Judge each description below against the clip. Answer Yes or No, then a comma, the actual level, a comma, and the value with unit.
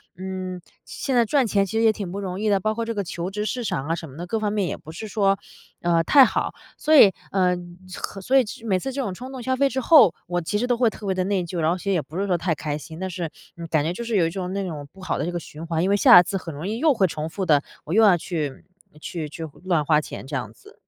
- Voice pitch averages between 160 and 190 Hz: Yes, medium, 185 Hz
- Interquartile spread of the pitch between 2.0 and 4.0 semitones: No, average, 4.4 semitones